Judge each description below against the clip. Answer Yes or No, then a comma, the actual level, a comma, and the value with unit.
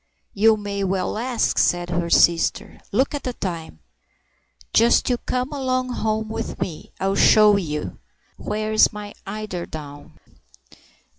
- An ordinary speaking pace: No, slow, 130 wpm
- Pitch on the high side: Yes, high, 210 Hz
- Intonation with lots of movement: No, average, 4.7 semitones